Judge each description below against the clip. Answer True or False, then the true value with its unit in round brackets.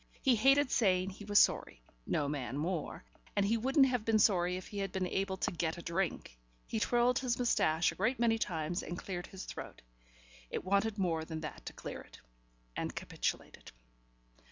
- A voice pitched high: True (195 Hz)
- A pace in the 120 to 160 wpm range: False (190 wpm)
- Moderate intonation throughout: True (4.5 semitones)